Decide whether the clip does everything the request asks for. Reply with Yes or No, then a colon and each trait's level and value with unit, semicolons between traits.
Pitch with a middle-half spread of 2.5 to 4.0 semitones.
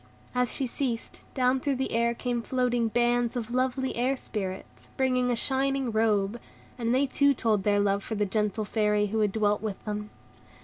Yes: average, 3.3 semitones